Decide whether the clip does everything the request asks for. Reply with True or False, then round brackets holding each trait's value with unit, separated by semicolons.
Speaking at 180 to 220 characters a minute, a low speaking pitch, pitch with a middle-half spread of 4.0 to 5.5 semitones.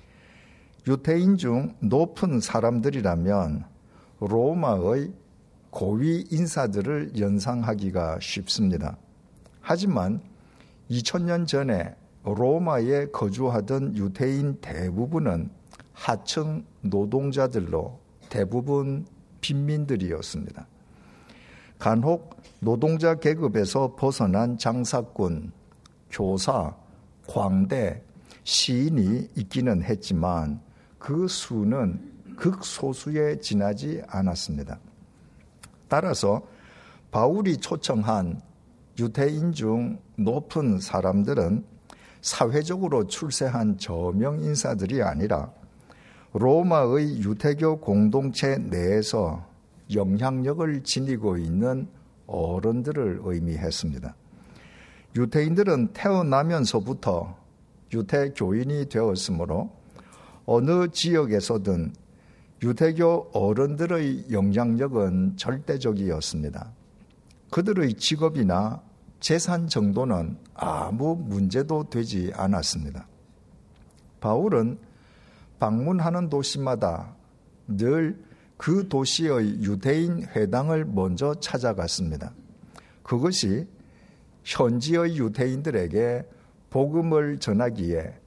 False (205 characters per minute; 125 Hz; 7.0 semitones)